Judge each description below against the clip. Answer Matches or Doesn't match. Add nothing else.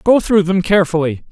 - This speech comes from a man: Matches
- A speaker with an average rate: Matches